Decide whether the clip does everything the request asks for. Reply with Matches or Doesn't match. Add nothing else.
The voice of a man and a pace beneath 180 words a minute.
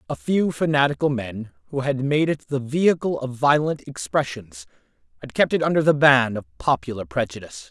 Matches